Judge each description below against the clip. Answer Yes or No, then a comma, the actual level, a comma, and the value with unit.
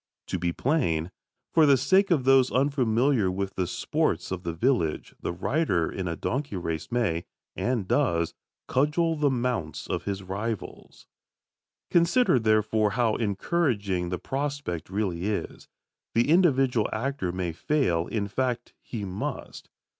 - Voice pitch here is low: Yes, low, 110 Hz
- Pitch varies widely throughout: Yes, wide, 6.7 semitones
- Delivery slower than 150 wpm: Yes, average, 140 wpm